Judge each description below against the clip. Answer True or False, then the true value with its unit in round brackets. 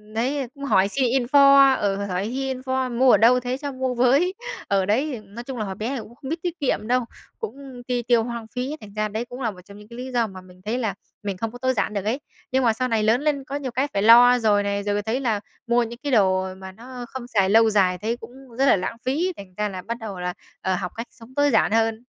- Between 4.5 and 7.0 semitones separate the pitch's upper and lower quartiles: False (3.9 semitones)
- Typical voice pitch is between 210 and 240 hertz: True (235 Hz)